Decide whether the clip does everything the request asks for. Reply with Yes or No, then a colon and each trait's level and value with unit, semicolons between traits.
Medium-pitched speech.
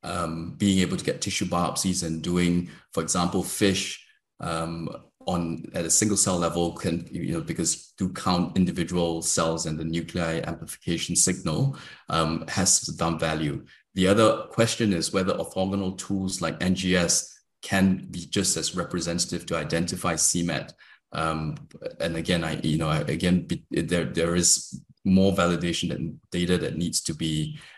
No: very low, 85 Hz